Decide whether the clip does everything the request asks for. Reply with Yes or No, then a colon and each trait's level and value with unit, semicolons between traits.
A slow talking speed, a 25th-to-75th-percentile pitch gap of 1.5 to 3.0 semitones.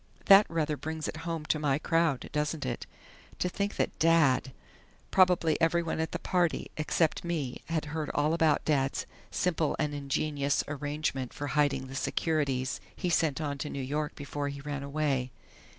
No: average, 165 wpm; narrow, 2.5 semitones